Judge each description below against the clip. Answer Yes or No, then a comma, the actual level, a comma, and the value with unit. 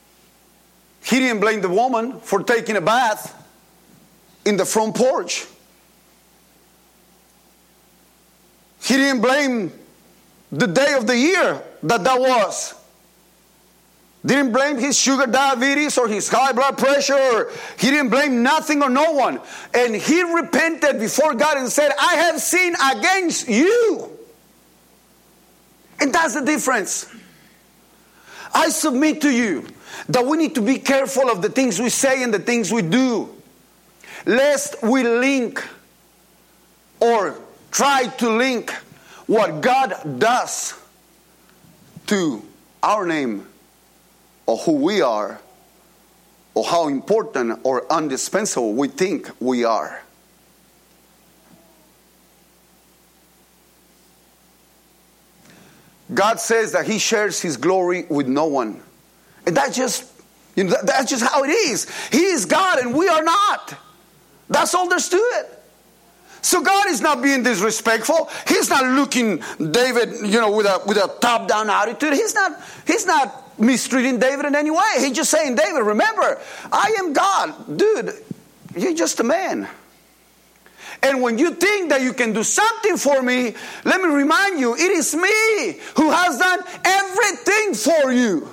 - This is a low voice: No, very high, 270 Hz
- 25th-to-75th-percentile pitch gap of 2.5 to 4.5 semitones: No, average, 5.3 semitones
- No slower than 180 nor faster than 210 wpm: No, slow, 135 wpm